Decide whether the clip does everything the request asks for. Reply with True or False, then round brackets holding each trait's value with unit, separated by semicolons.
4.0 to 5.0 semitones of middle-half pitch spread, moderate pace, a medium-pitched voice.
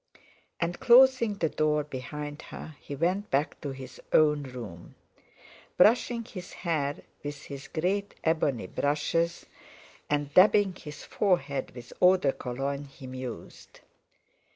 False (4.6 semitones; 130 wpm; 150 Hz)